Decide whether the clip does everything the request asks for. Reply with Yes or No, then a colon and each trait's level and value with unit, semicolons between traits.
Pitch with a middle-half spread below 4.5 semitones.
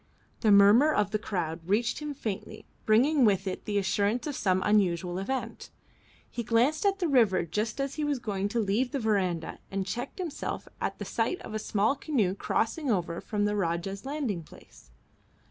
No: average, 5.1 semitones